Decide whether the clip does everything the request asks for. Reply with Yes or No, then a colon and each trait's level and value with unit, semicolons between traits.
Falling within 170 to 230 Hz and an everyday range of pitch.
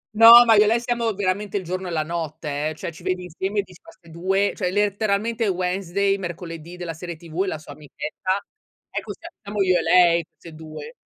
Yes: medium, 185 Hz; average, 3.3 semitones